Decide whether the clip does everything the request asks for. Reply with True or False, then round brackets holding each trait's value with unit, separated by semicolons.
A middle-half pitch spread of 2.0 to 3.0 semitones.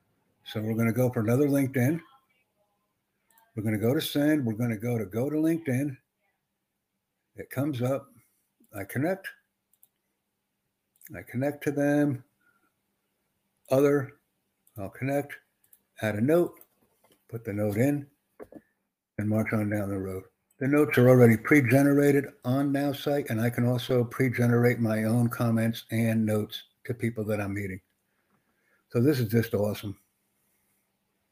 False (4.4 semitones)